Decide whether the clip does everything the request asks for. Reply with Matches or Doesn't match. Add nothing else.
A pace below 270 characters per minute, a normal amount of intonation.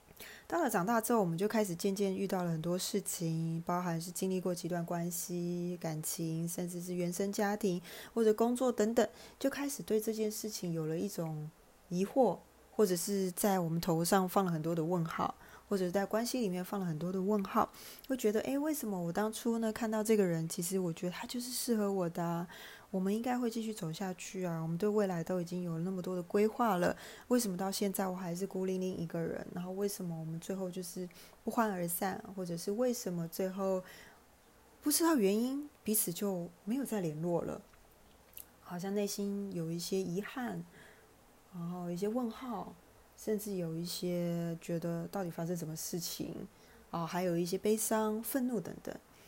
Doesn't match